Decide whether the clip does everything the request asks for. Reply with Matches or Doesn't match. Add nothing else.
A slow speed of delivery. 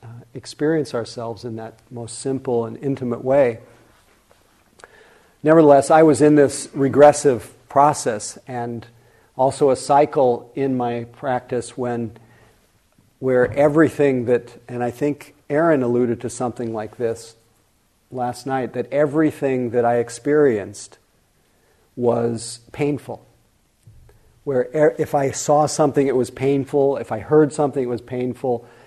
Matches